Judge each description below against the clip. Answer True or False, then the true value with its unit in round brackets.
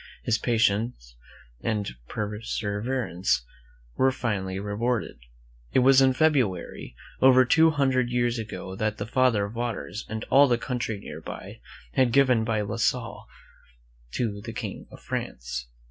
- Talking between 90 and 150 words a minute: True (140 wpm)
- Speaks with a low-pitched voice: True (115 Hz)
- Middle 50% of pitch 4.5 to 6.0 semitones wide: False (3.7 semitones)